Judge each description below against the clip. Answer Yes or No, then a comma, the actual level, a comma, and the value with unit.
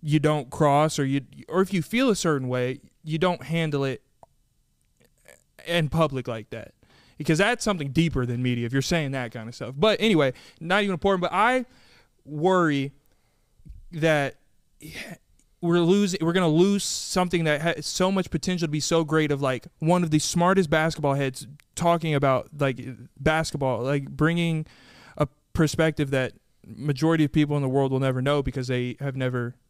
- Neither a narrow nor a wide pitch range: Yes, average, 4.3 semitones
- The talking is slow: No, average, 175 wpm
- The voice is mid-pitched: Yes, medium, 150 Hz